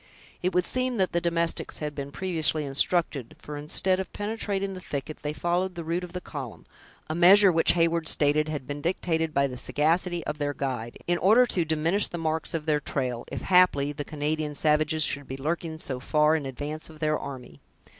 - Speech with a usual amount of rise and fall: Yes, average, 3.2 semitones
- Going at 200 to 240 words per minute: Yes, fast, 205 wpm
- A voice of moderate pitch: Yes, medium, 155 Hz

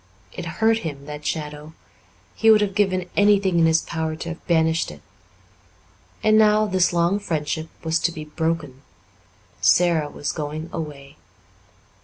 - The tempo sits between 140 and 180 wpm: Yes, average, 150 wpm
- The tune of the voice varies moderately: Yes, average, 3.7 semitones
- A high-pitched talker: No, medium, 165 Hz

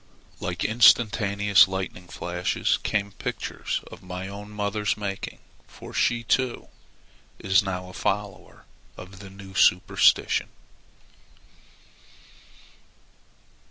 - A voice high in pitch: No, low, 100 Hz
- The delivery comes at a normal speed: No, slow, 95 wpm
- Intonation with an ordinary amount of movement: No, narrow, 2.0 semitones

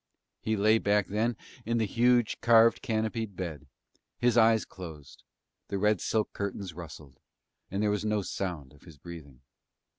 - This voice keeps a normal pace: Yes, average, 155 wpm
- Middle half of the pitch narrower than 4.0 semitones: No, average, 4.4 semitones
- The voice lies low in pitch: Yes, low, 105 Hz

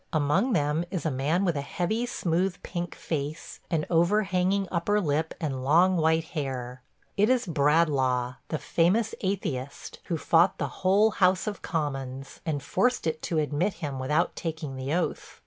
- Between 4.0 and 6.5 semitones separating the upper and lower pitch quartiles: Yes, average, 4.4 semitones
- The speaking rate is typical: Yes, average, 165 wpm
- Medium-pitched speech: Yes, medium, 165 Hz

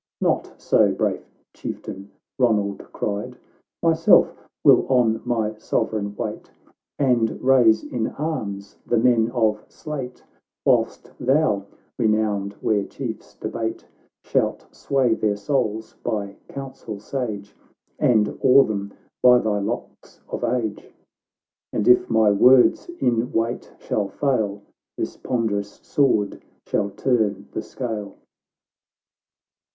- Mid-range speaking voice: No, low, 110 Hz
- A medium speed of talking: No, slow, 120 wpm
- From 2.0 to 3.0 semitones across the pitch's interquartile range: No, average, 3.4 semitones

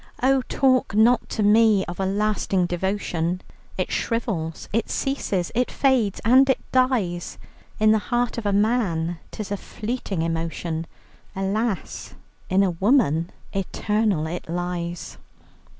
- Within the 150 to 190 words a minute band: No, slow, 135 wpm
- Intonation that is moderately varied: Yes, average, 4.8 semitones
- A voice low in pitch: No, high, 200 Hz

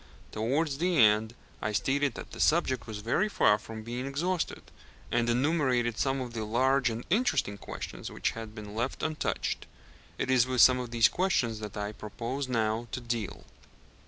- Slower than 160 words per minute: No, average, 175 wpm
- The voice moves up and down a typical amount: Yes, average, 3.7 semitones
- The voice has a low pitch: Yes, low, 120 Hz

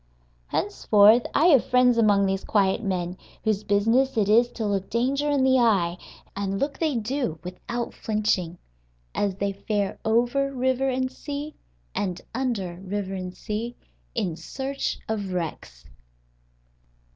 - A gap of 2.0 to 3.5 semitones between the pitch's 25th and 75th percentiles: No, average, 4.9 semitones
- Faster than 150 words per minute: No, average, 140 wpm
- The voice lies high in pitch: Yes, high, 215 Hz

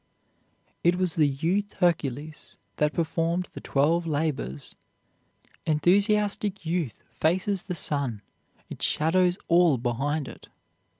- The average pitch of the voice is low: No, medium, 165 Hz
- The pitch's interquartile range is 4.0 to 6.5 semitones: No, average, 3.6 semitones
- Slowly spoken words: Yes, slow, 110 wpm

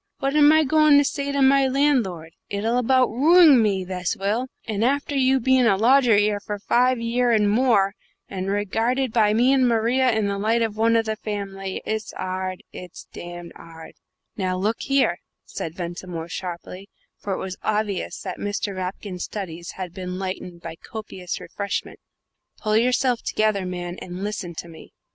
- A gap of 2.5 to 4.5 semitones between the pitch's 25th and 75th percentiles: No, average, 5.0 semitones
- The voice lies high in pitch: Yes, high, 210 Hz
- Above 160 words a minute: Yes, average, 175 wpm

